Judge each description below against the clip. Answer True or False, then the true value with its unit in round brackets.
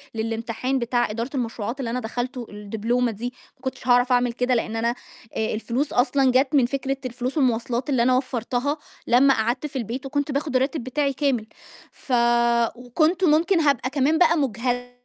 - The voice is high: True (250 Hz)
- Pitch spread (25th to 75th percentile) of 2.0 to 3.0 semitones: True (2.7 semitones)